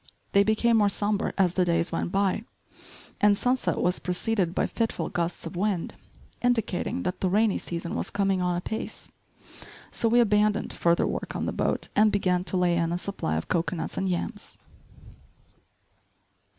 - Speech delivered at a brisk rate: No, average, 165 wpm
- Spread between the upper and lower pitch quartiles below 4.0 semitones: Yes, average, 3.2 semitones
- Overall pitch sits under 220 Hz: Yes, high, 190 Hz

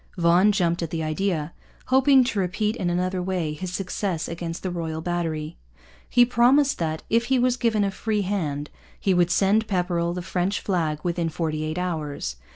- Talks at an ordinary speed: Yes, average, 180 wpm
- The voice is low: No, medium, 180 Hz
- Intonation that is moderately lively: Yes, average, 3.8 semitones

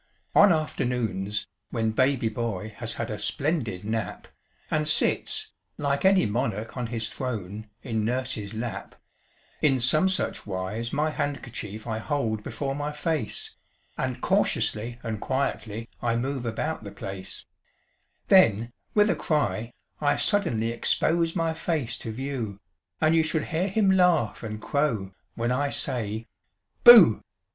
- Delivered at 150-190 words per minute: No, average, 140 wpm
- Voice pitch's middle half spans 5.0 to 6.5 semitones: Yes, wide, 5.4 semitones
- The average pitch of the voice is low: Yes, low, 120 Hz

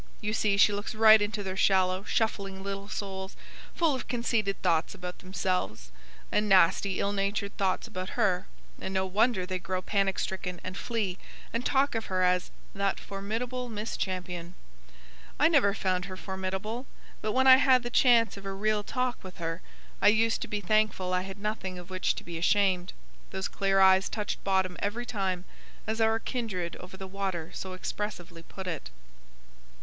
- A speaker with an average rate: Yes, average, 180 wpm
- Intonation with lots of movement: No, average, 2.7 semitones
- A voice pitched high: Yes, high, 195 Hz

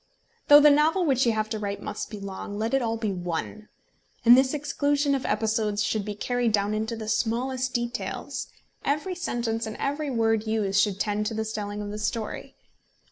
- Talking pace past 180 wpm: Yes, average, 195 wpm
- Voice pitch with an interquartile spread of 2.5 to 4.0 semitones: Yes, average, 3.7 semitones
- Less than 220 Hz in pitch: No, high, 225 Hz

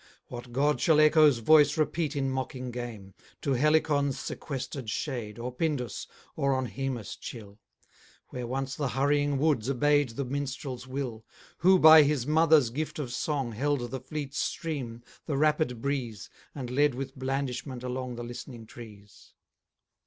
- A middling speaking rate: Yes, average, 150 wpm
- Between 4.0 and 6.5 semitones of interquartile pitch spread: No, average, 3.3 semitones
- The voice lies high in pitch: No, low, 135 Hz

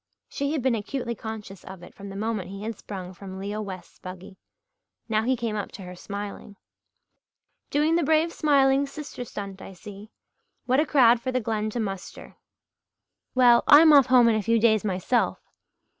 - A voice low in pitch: No, high, 220 Hz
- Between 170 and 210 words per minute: Yes, average, 185 wpm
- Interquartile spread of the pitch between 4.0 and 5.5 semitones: Yes, average, 4.5 semitones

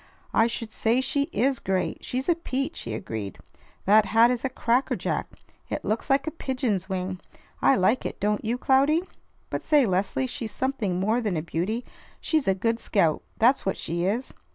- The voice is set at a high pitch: Yes, high, 230 Hz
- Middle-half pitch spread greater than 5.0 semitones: Yes, wide, 5.5 semitones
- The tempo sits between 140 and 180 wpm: No, average, 190 wpm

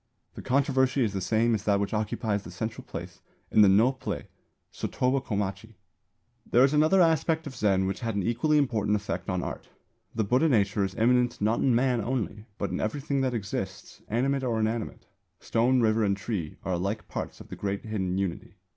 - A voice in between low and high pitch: No, low, 110 Hz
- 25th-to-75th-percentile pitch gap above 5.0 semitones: No, average, 4.2 semitones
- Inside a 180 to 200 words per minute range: Yes, average, 195 wpm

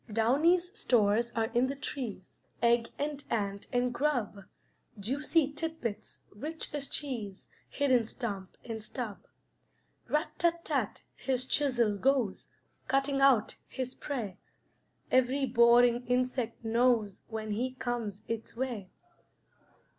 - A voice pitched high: Yes, high, 245 Hz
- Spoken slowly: Yes, slow, 120 wpm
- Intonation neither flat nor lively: Yes, average, 3.6 semitones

